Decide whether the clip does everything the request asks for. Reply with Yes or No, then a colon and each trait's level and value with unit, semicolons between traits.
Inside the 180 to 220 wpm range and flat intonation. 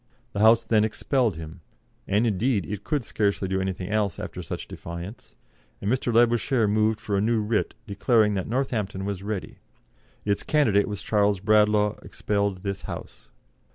No: average, 160 wpm; narrow, 2.2 semitones